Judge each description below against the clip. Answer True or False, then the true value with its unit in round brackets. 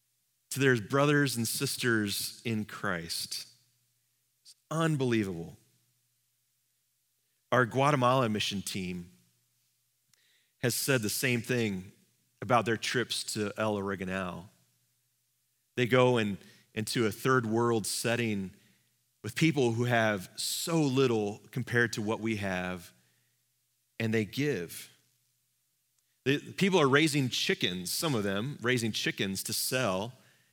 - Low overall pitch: True (120 Hz)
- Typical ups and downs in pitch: True (3.1 semitones)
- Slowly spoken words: True (115 wpm)